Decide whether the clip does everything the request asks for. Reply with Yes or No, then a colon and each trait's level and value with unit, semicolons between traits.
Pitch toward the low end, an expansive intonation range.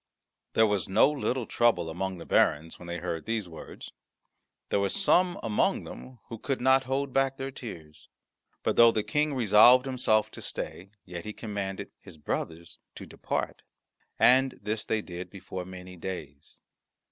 Yes: low, 105 Hz; wide, 6.2 semitones